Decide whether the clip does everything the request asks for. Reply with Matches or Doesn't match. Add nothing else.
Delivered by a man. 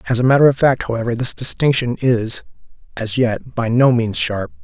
Matches